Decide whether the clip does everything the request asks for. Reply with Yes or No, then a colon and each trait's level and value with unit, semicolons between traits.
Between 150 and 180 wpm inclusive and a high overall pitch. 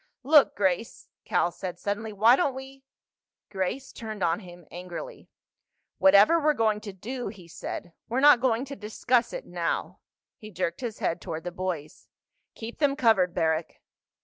Yes: average, 160 wpm; high, 215 Hz